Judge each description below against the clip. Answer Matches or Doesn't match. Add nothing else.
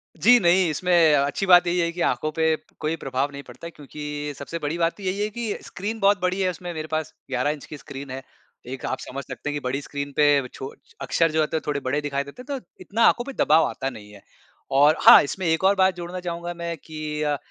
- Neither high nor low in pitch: Matches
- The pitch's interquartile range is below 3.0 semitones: Doesn't match